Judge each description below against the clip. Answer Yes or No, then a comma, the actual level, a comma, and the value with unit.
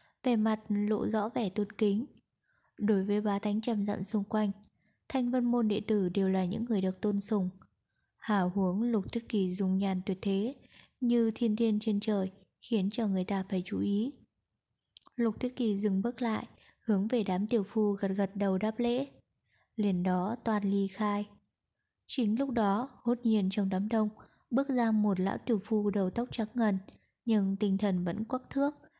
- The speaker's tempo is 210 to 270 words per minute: No, average, 190 wpm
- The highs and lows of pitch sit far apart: No, narrow, 2.6 semitones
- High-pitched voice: Yes, high, 210 Hz